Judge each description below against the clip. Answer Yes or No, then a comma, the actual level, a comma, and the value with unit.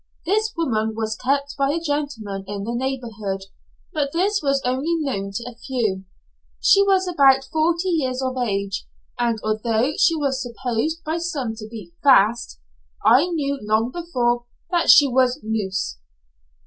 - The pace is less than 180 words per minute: Yes, average, 155 wpm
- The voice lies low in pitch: No, very high, 255 Hz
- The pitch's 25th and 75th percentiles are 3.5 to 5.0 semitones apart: No, wide, 5.5 semitones